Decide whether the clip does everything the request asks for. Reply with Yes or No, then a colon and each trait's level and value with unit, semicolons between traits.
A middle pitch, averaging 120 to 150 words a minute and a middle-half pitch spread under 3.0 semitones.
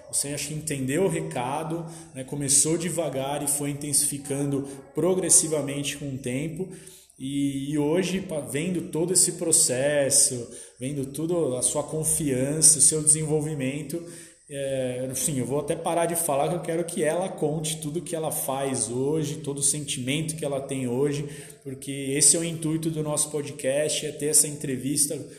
No: medium, 145 Hz; average, 160 wpm; narrow, 2.5 semitones